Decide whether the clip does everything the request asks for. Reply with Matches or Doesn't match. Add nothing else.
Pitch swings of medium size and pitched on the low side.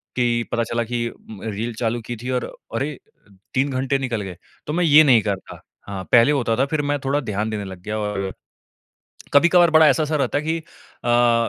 Matches